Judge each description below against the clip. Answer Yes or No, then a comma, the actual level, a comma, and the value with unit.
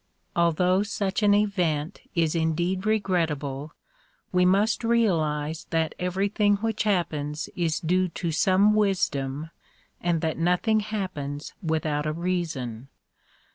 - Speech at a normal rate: No, slow, 115 wpm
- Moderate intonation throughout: Yes, average, 4.2 semitones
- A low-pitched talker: No, medium, 175 Hz